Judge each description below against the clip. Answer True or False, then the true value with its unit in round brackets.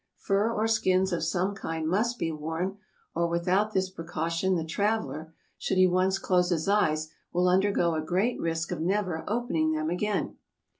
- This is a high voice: False (180 Hz)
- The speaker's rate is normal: True (170 wpm)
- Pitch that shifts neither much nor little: True (3.4 semitones)